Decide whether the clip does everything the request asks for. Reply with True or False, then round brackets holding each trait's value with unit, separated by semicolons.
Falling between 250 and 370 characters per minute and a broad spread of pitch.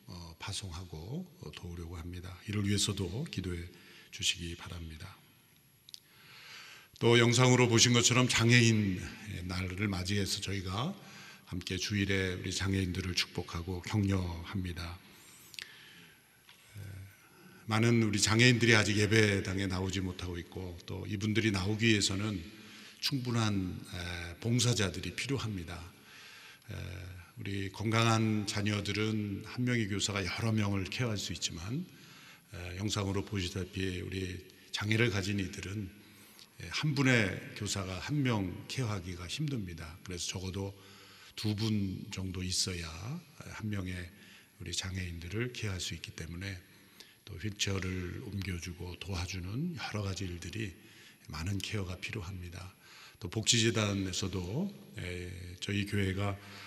False (270 characters per minute; 3.1 semitones)